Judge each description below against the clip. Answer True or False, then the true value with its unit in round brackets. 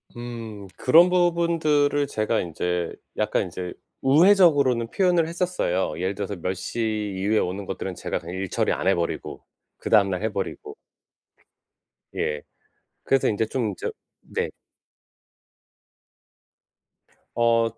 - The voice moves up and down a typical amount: False (7.4 semitones)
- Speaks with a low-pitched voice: True (110 Hz)